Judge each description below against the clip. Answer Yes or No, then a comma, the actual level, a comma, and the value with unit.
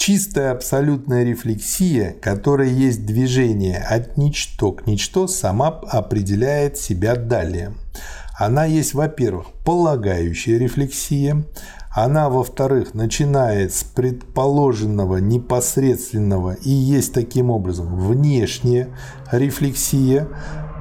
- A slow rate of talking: Yes, slow, 90 wpm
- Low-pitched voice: Yes, low, 125 Hz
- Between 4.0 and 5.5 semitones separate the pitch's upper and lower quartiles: Yes, average, 4.7 semitones